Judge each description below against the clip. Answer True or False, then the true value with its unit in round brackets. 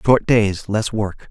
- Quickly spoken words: False (185 wpm)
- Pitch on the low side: True (105 Hz)